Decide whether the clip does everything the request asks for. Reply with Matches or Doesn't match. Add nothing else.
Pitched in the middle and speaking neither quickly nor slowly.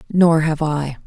Matches